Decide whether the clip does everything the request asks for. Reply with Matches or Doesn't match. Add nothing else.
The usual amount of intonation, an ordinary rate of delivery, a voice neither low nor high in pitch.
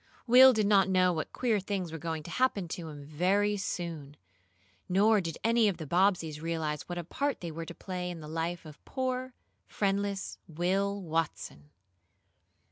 Matches